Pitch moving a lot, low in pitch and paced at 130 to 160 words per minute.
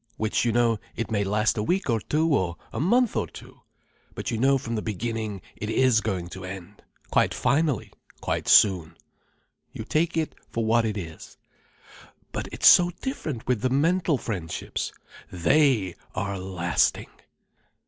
Yes: wide, 6.0 semitones; low, 115 Hz; average, 155 wpm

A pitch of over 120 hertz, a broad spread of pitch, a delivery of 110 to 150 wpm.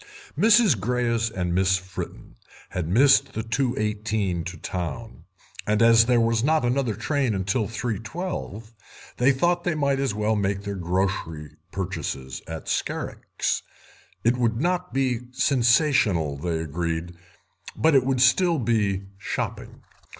No: low, 115 Hz; wide, 5.7 semitones; slow, 135 wpm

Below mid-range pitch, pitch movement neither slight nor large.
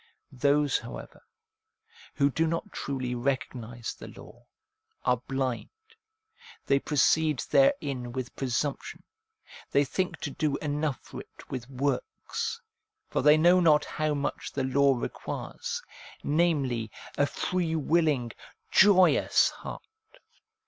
No: medium, 145 Hz; average, 3.5 semitones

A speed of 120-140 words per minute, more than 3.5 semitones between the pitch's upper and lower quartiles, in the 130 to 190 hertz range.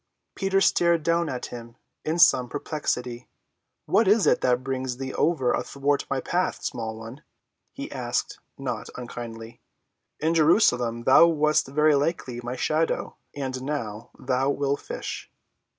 Yes: slow, 135 wpm; average, 4.1 semitones; low, 135 Hz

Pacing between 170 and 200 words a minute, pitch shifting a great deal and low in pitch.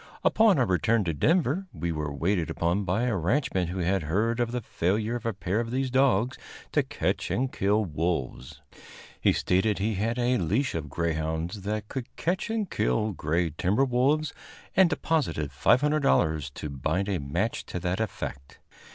Yes: average, 175 wpm; wide, 6.7 semitones; low, 100 Hz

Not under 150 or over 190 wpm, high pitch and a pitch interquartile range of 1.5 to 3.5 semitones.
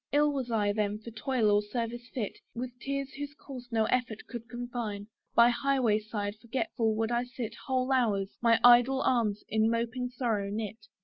Yes: average, 185 wpm; high, 235 Hz; average, 2.8 semitones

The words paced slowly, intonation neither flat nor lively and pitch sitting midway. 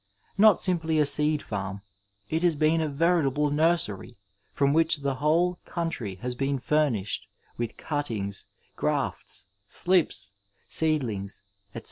No: slow, 130 wpm; wide, 5.7 semitones; medium, 150 Hz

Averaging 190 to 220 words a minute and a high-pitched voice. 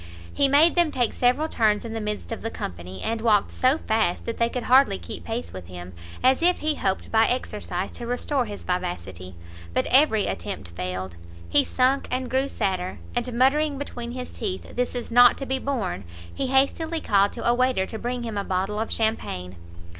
Yes: average, 200 wpm; high, 230 Hz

